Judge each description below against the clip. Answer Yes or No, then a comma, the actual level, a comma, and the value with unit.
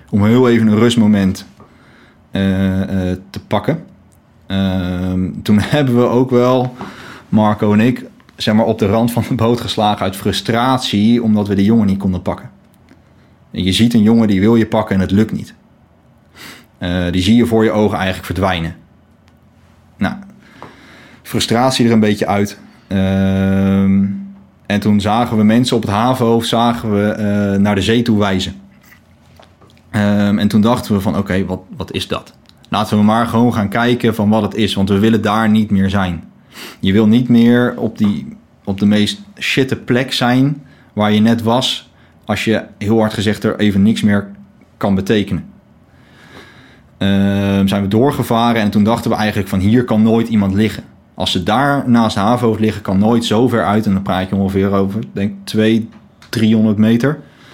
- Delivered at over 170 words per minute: Yes, average, 180 wpm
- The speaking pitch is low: Yes, low, 105 Hz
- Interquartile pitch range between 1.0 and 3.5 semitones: Yes, average, 2.8 semitones